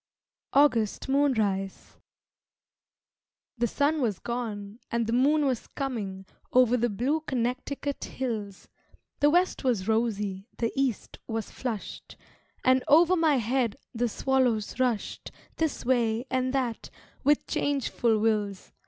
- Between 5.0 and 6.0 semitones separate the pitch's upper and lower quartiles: No, average, 3.6 semitones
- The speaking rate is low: Yes, slow, 120 wpm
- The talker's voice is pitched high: Yes, high, 245 Hz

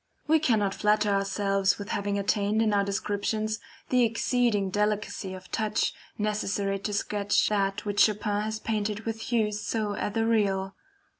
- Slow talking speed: No, average, 145 wpm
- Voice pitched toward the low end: No, high, 210 Hz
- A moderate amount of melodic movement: No, narrow, 1.4 semitones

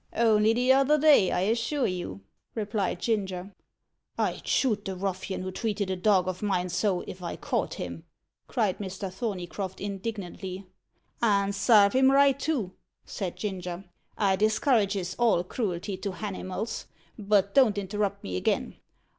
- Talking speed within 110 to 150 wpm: Yes, average, 140 wpm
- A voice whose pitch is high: Yes, high, 200 Hz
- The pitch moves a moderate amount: Yes, average, 3.0 semitones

